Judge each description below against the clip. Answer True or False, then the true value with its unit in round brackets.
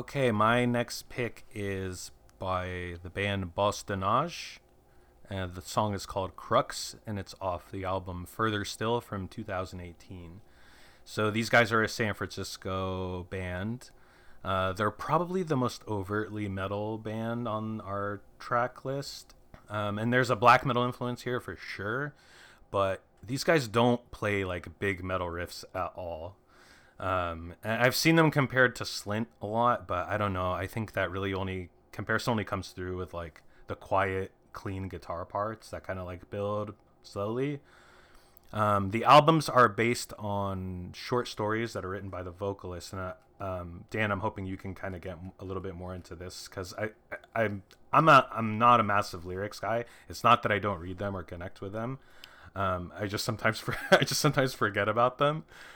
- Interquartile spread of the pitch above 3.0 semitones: True (4.0 semitones)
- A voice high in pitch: False (100 Hz)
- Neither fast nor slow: True (180 wpm)